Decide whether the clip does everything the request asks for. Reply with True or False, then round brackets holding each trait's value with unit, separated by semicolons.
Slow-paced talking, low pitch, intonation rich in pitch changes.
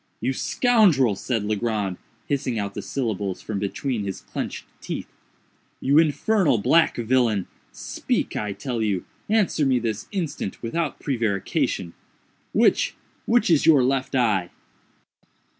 True (110 wpm; 120 Hz; 5.9 semitones)